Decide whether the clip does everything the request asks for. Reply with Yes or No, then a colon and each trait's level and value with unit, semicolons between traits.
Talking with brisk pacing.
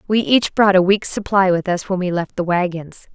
Yes: fast, 250 wpm